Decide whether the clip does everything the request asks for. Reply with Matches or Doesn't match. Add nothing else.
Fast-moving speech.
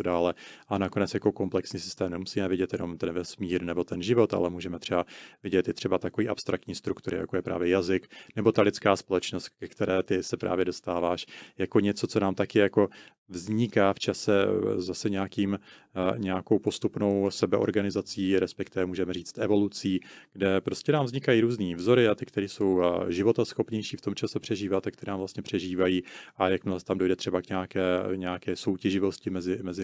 Matches